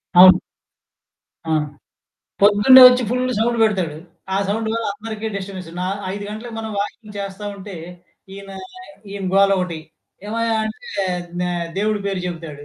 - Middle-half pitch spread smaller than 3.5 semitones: Yes, average, 2.9 semitones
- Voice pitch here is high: Yes, high, 205 Hz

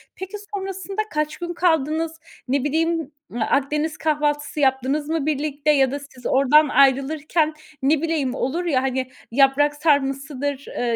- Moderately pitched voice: No, very high, 295 Hz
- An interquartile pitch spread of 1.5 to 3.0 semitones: Yes, average, 2.7 semitones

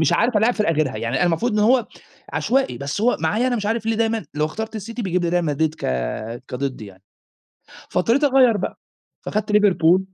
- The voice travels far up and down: Yes, wide, 6.9 semitones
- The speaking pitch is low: No, high, 205 Hz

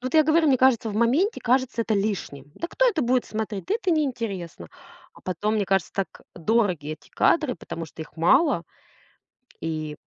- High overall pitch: Yes, high, 220 Hz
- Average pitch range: No, wide, 7.3 semitones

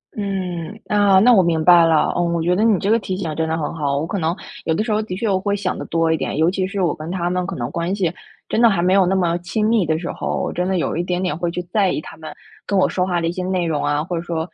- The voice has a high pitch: No, medium, 180 Hz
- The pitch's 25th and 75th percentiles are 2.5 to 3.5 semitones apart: Yes, average, 2.8 semitones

